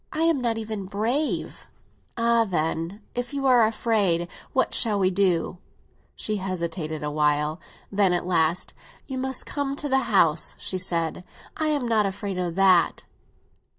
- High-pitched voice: Yes, high, 200 Hz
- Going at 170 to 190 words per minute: No, average, 150 wpm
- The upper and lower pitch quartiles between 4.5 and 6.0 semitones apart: Yes, wide, 5.5 semitones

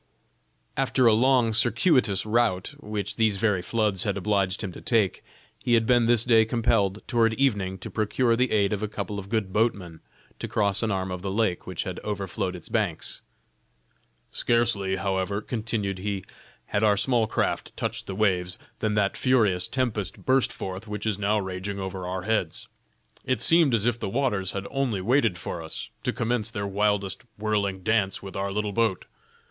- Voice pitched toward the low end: Yes, low, 105 Hz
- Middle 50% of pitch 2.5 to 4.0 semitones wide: Yes, average, 3.0 semitones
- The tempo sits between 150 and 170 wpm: No, average, 180 wpm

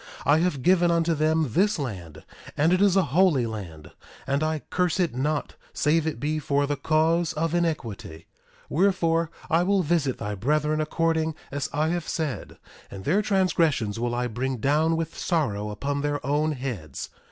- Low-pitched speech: No, medium, 155 Hz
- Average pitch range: Yes, average, 4.1 semitones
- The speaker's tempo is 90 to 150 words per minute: No, average, 175 wpm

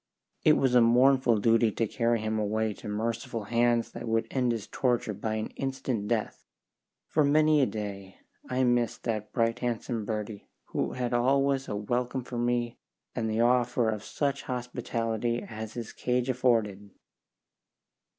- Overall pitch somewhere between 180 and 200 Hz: No, low, 120 Hz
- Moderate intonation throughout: No, narrow, 2.3 semitones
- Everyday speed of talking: Yes, average, 160 wpm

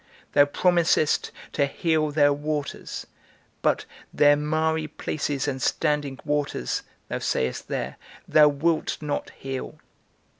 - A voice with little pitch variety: Yes, narrow, 1.5 semitones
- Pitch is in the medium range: Yes, medium, 150 Hz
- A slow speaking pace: Yes, slow, 115 wpm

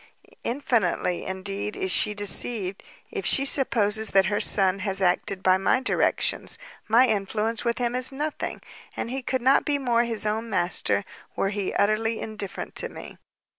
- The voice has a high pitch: Yes, high, 215 Hz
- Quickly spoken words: No, average, 165 wpm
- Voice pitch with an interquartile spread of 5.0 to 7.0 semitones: No, average, 3.8 semitones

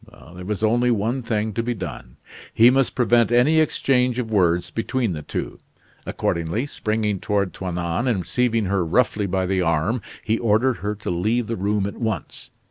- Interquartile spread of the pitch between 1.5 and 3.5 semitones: No, average, 4.3 semitones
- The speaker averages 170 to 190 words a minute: Yes, average, 180 wpm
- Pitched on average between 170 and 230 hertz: No, low, 110 Hz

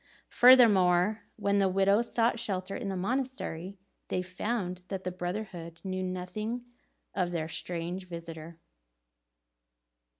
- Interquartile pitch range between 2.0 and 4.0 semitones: Yes, average, 3.2 semitones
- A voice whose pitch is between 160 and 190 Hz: Yes, medium, 185 Hz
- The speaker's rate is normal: No, slow, 120 wpm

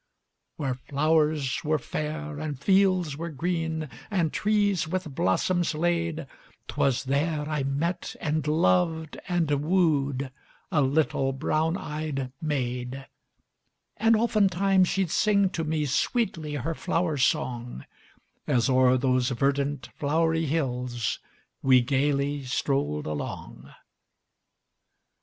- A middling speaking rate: No, slow, 110 wpm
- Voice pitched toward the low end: No, medium, 150 Hz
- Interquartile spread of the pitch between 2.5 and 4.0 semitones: Yes, average, 3.6 semitones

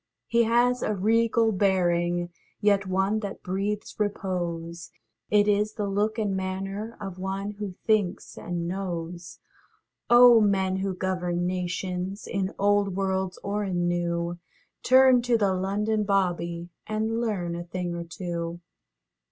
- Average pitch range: Yes, average, 3.0 semitones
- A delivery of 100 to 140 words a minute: Yes, slow, 135 wpm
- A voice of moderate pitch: No, high, 195 Hz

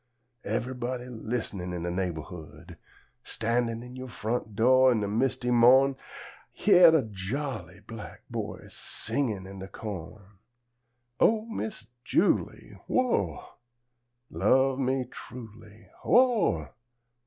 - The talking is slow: Yes, slow, 115 wpm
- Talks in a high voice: No, low, 115 Hz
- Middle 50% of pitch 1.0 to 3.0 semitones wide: No, average, 4.7 semitones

